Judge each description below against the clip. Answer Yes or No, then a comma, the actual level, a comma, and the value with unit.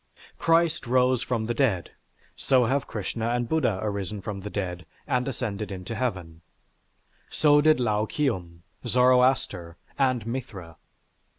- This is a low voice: Yes, low, 115 Hz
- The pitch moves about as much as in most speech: Yes, average, 4.5 semitones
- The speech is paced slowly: Yes, slow, 130 wpm